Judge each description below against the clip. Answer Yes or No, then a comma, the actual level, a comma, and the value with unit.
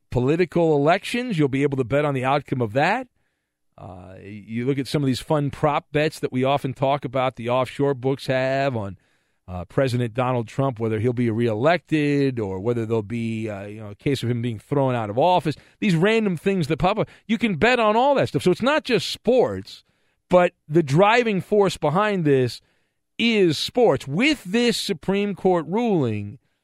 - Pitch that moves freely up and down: Yes, wide, 6.8 semitones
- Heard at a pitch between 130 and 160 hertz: Yes, medium, 140 Hz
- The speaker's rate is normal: Yes, average, 195 wpm